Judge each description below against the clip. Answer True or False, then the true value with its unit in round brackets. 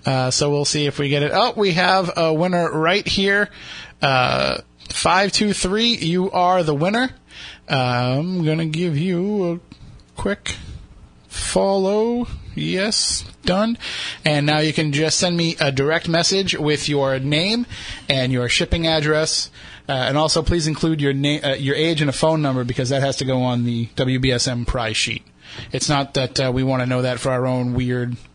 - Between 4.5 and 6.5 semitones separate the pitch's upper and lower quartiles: True (5.0 semitones)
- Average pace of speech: True (185 wpm)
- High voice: False (150 Hz)